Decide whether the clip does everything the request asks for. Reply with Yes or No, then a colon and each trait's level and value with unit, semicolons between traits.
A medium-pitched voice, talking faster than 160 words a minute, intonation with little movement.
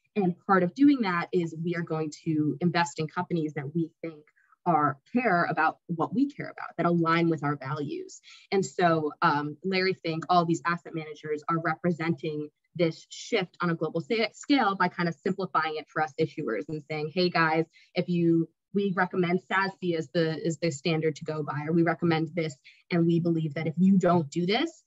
Yes: medium, 170 Hz; average, 200 wpm; narrow, 2.2 semitones